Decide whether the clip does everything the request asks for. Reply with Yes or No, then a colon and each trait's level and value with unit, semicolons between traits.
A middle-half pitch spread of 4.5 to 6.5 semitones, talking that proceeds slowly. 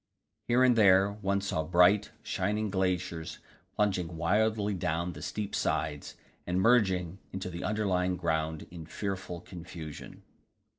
No: average, 3.2 semitones; slow, 130 wpm